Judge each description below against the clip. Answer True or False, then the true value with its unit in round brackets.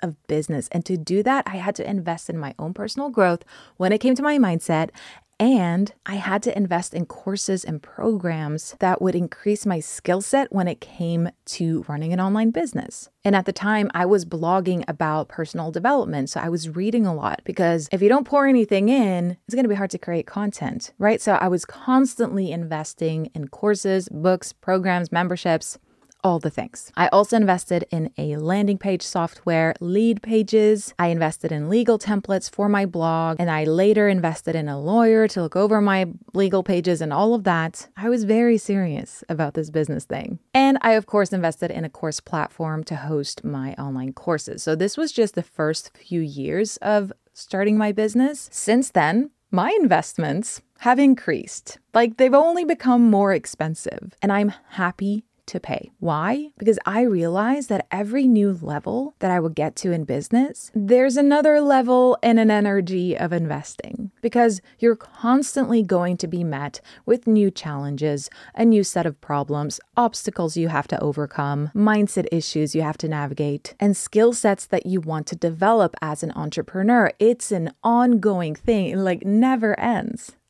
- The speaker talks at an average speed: True (180 wpm)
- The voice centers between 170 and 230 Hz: True (190 Hz)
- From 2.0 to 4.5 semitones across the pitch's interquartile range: False (5.1 semitones)